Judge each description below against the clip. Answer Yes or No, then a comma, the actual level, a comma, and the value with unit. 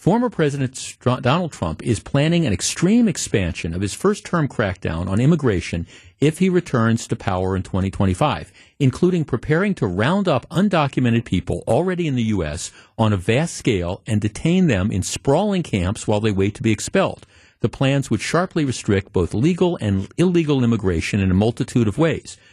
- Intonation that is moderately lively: No, wide, 7.9 semitones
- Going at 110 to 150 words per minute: No, average, 175 wpm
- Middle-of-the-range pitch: No, low, 120 Hz